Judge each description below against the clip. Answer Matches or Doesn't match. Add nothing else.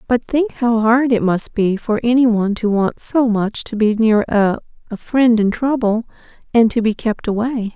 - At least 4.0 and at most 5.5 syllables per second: Matches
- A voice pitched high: Matches